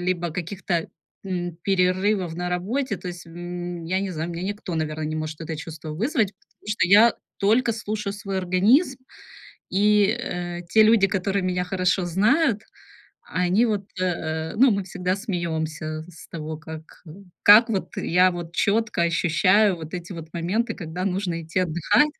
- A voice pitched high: No, medium, 180 Hz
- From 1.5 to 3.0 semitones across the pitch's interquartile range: No, average, 3.4 semitones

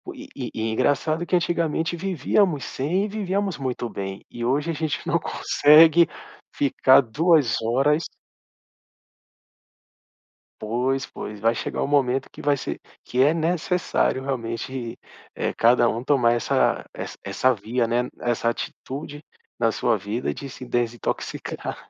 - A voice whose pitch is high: No, low, 135 Hz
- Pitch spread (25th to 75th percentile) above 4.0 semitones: Yes, average, 5.2 semitones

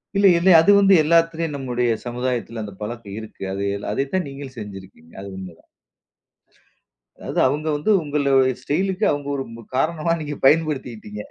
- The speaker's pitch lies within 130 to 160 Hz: Yes, low, 135 Hz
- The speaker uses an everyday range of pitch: No, wide, 5.7 semitones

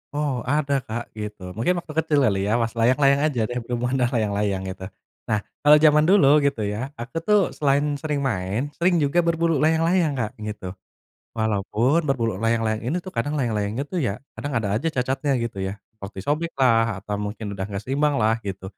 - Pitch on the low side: Yes, low, 125 Hz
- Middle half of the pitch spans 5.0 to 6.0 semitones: Yes, wide, 5.6 semitones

